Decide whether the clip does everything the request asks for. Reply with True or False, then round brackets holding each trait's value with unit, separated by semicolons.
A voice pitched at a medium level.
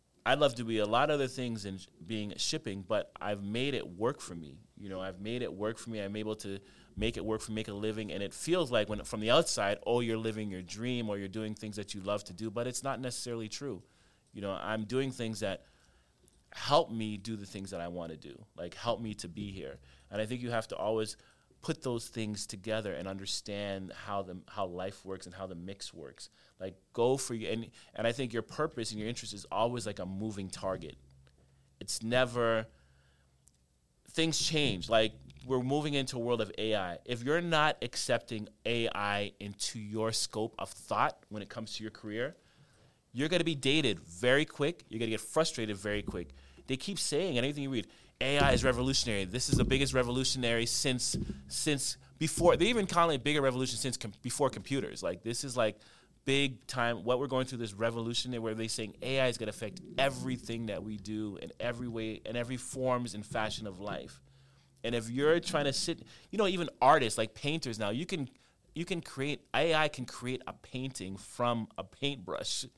False (115 Hz)